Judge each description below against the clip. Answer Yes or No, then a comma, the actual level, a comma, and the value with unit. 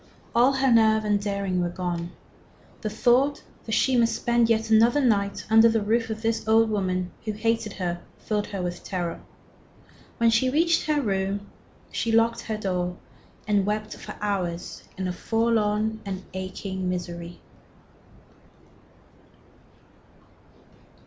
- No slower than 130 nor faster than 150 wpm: Yes, average, 140 wpm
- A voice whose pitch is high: Yes, high, 215 Hz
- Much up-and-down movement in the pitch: No, average, 3.3 semitones